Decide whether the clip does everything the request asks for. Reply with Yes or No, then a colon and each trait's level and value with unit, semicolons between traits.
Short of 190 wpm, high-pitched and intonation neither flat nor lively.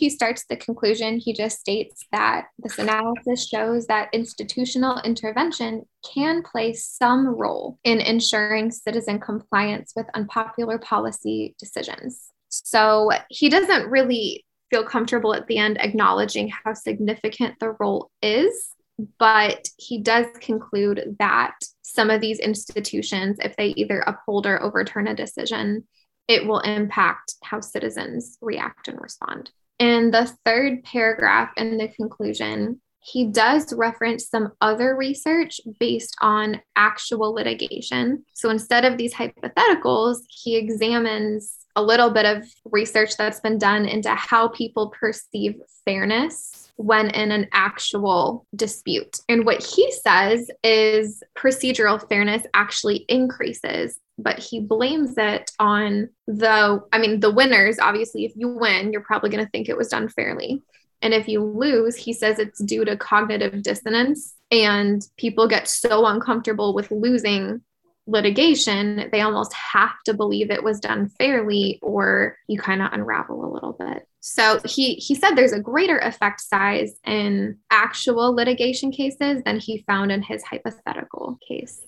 No: average, 145 wpm; high, 220 Hz; narrow, 2.2 semitones